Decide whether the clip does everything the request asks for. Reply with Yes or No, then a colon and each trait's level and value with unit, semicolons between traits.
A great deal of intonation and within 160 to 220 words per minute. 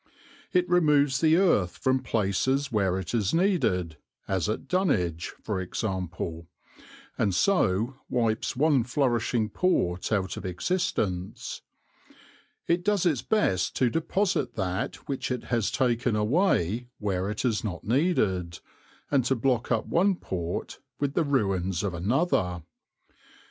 No: wide, 7.5 semitones; slow, 135 wpm